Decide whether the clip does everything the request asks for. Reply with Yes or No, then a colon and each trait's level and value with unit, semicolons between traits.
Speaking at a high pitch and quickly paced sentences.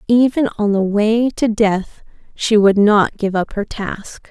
No: high, 210 Hz; average, 180 wpm